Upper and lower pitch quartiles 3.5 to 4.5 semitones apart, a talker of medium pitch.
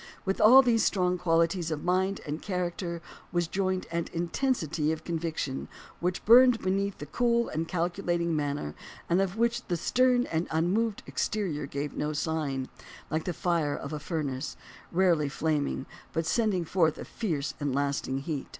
Yes: average, 4.0 semitones; medium, 170 Hz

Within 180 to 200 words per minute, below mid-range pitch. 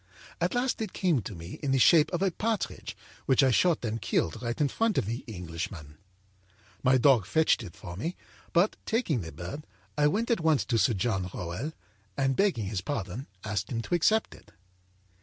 Yes: average, 195 wpm; low, 130 Hz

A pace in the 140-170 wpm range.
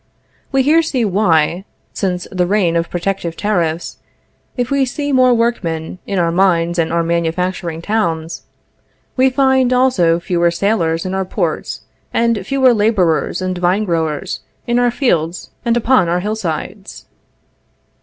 Yes: average, 145 wpm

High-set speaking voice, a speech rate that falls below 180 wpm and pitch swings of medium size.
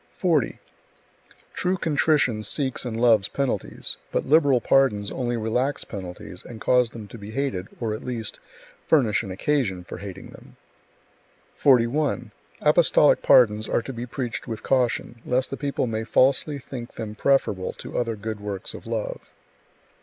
No: low, 120 Hz; average, 155 wpm; average, 4.1 semitones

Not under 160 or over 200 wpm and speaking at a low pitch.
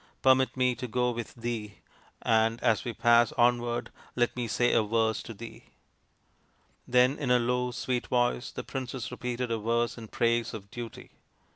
Yes: average, 170 wpm; low, 120 Hz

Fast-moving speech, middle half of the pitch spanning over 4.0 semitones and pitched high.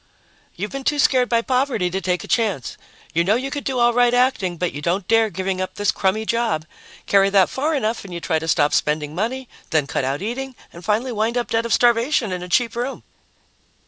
Yes: fast, 230 wpm; wide, 5.4 semitones; high, 220 Hz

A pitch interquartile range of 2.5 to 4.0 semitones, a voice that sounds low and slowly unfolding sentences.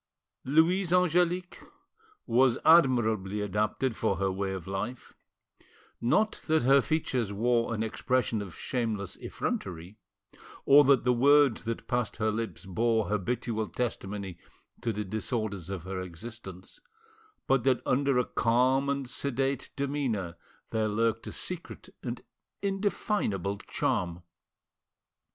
No: average, 5.0 semitones; low, 115 Hz; slow, 125 wpm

